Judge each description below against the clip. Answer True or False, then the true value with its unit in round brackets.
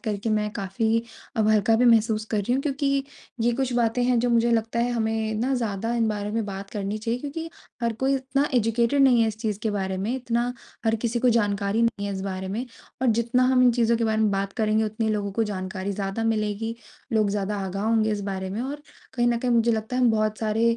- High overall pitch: True (225 Hz)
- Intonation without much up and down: True (2.3 semitones)